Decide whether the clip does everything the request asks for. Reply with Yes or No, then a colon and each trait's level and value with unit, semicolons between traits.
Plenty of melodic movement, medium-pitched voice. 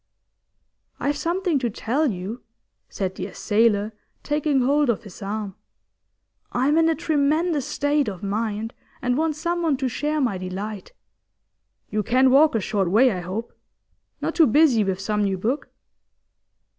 No: wide, 6.3 semitones; high, 245 Hz